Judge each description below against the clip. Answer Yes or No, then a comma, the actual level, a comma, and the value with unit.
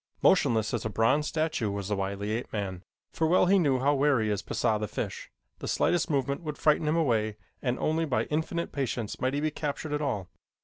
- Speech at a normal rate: No, fast, 215 wpm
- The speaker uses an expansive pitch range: Yes, wide, 6.1 semitones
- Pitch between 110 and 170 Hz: Yes, low, 135 Hz